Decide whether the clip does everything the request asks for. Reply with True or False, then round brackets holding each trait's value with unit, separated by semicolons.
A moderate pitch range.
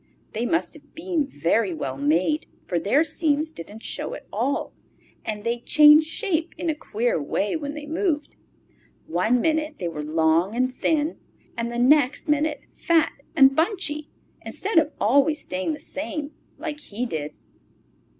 False (6.9 semitones)